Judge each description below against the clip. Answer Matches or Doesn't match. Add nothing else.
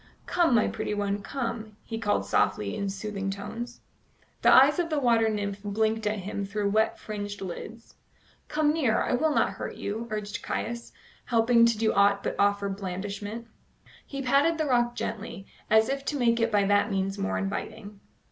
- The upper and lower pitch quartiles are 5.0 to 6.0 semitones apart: Doesn't match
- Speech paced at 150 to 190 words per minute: Matches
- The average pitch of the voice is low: Doesn't match